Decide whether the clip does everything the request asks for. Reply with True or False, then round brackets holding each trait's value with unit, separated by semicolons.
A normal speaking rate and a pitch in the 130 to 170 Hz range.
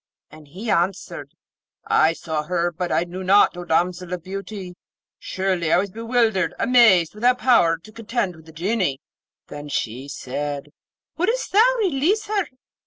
False (155 wpm; 185 Hz)